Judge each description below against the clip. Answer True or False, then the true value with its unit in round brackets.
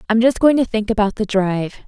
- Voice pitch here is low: False (220 Hz)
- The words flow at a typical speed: False (255 wpm)